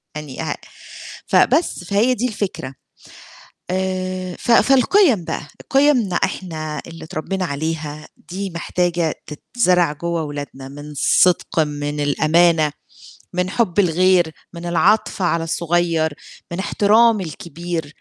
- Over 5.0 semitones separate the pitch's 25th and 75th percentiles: No, average, 3.4 semitones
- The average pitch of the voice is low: No, medium, 175 Hz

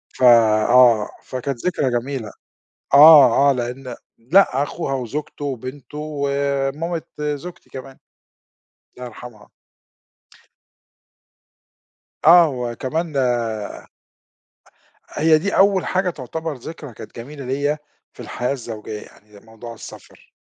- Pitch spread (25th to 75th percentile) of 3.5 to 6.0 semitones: Yes, average, 3.9 semitones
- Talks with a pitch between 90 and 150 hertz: Yes, low, 135 Hz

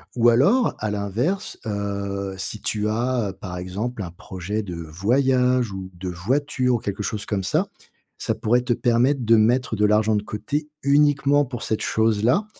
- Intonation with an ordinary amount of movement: Yes, average, 4.1 semitones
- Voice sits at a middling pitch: No, low, 110 Hz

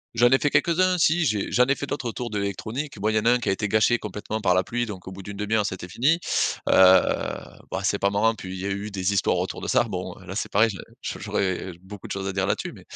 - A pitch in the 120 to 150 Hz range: No, low, 105 Hz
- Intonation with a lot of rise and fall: No, average, 3.7 semitones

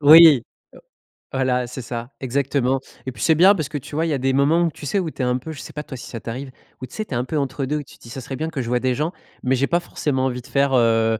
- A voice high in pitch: No, low, 135 Hz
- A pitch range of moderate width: Yes, average, 3.1 semitones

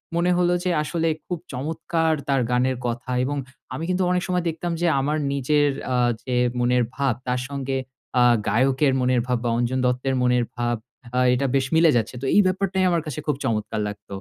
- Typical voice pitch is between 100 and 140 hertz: Yes, low, 135 Hz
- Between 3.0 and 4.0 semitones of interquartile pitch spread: No, average, 4.7 semitones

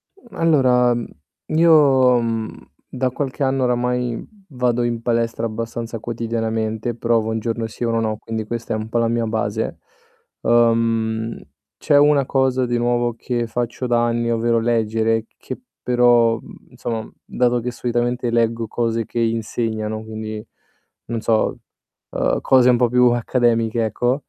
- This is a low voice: Yes, low, 115 Hz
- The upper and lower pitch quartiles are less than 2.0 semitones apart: Yes, narrow, 1.4 semitones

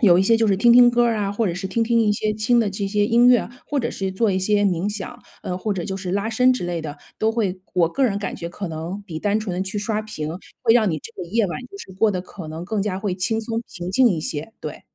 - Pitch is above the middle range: Yes, high, 205 Hz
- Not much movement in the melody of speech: No, average, 3.6 semitones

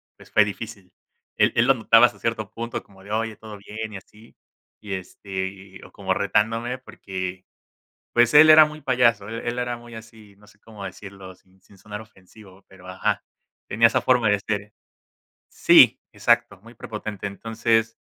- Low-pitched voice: Yes, low, 110 Hz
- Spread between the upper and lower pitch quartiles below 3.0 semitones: Yes, narrow, 2.6 semitones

